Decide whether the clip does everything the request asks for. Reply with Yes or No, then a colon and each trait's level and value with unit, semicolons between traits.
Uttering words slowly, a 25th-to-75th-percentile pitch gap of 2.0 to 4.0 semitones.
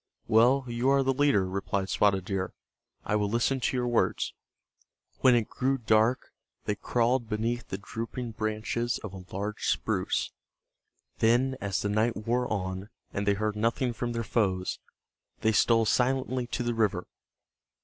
No: average, 160 wpm; average, 3.0 semitones